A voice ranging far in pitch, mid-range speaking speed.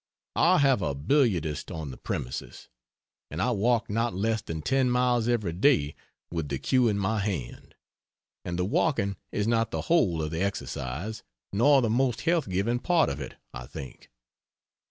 Yes: wide, 6.8 semitones; average, 175 wpm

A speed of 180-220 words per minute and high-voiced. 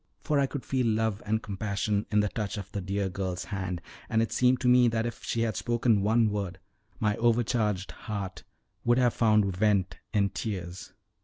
No: average, 190 wpm; low, 105 Hz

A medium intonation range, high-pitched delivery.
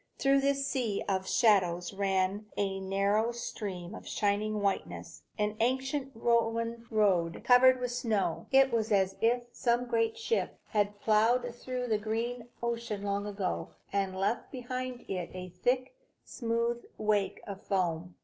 Yes: average, 3.6 semitones; high, 220 Hz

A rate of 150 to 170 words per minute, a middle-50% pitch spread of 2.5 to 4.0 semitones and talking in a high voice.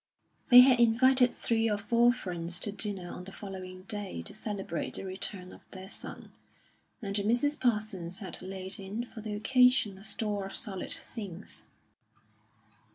Yes: average, 160 wpm; average, 3.2 semitones; high, 205 Hz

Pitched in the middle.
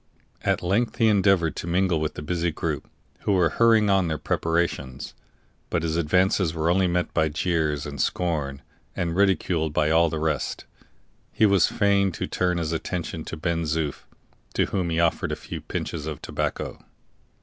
No: very low, 85 Hz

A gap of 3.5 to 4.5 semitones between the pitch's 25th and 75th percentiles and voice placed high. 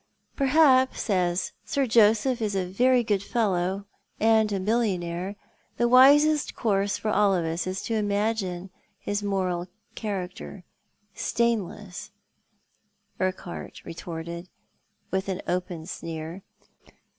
Yes: average, 3.8 semitones; high, 200 Hz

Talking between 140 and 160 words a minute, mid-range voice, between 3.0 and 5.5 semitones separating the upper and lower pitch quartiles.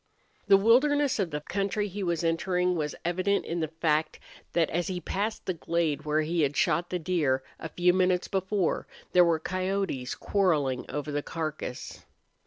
No: average, 175 wpm; medium, 175 Hz; average, 3.5 semitones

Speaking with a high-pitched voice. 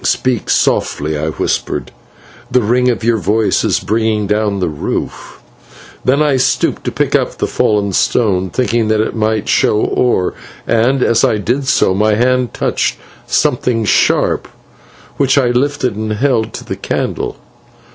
No: low, 110 Hz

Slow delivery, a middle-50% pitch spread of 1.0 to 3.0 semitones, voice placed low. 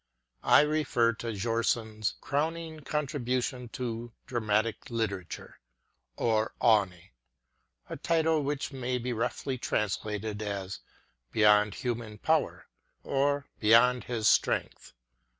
No: slow, 110 wpm; average, 4.0 semitones; low, 115 Hz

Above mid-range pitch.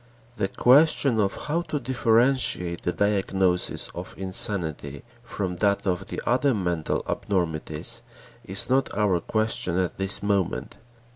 No: low, 100 Hz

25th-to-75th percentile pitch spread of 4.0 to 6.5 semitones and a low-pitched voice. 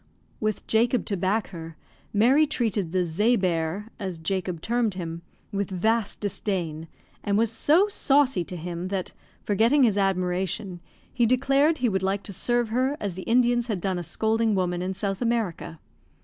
No: average, 4.4 semitones; high, 200 Hz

